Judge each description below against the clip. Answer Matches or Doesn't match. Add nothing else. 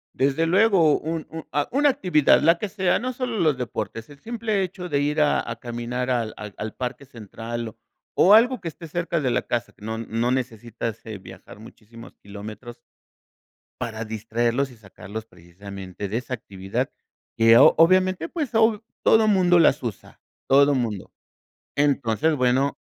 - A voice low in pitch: Matches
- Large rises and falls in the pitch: Matches